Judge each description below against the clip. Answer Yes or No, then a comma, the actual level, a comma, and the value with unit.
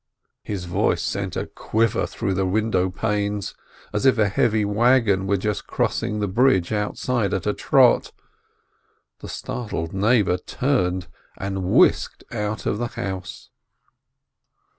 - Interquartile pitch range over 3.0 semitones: No, average, 2.7 semitones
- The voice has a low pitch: Yes, low, 105 Hz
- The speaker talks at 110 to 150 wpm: Yes, slow, 135 wpm